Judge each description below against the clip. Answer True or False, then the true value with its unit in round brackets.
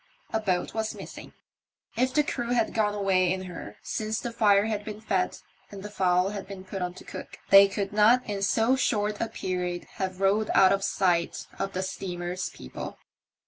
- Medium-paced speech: True (195 wpm)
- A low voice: False (200 Hz)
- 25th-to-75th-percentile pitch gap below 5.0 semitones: True (2.7 semitones)